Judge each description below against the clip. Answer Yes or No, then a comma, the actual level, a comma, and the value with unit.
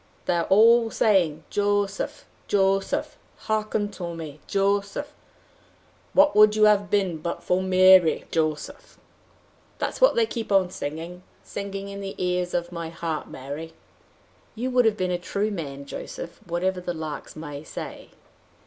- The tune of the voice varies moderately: Yes, average, 3.6 semitones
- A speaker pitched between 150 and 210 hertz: Yes, high, 190 Hz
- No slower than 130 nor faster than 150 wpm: Yes, slow, 135 wpm